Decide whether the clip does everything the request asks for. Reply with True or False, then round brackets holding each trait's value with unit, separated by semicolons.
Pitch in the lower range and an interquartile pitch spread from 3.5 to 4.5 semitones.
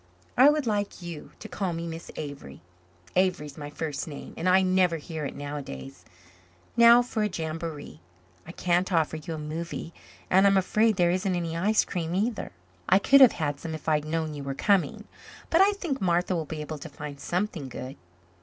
False (170 Hz; 4.2 semitones)